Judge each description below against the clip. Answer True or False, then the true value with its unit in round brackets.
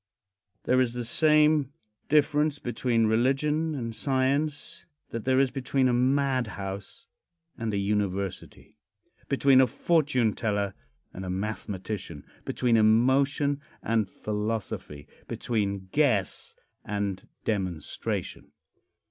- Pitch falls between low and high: False (120 Hz)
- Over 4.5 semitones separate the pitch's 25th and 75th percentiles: True (5.1 semitones)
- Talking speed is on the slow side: True (105 wpm)